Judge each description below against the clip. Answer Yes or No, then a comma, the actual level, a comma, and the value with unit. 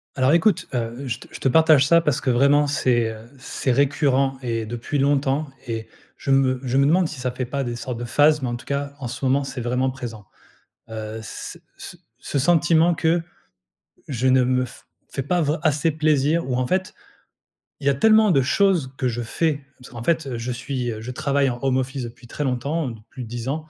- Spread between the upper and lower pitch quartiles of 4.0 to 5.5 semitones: No, average, 3.2 semitones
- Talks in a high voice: No, low, 135 Hz